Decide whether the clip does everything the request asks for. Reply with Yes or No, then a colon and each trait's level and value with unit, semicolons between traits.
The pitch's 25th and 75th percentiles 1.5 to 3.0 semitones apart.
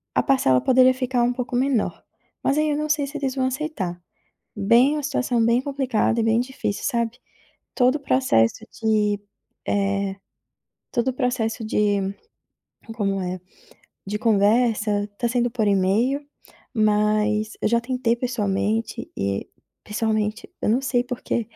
No: average, 3.5 semitones